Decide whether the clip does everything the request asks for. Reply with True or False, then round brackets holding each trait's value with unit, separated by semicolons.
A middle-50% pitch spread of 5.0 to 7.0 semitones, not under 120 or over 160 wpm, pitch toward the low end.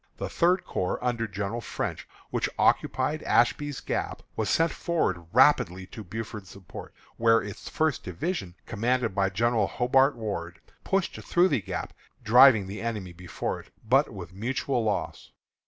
True (5.3 semitones; 150 wpm; 115 Hz)